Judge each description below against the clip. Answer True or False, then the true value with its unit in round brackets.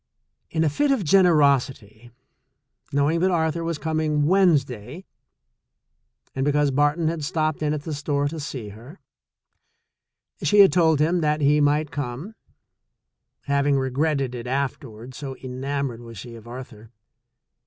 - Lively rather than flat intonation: False (3.4 semitones)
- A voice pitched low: False (145 Hz)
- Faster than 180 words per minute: False (145 wpm)